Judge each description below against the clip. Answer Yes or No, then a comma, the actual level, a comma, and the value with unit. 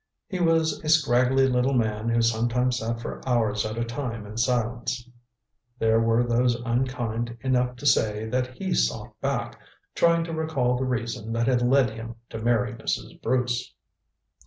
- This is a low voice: Yes, low, 120 Hz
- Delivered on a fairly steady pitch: Yes, narrow, 1.9 semitones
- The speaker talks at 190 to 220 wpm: No, average, 165 wpm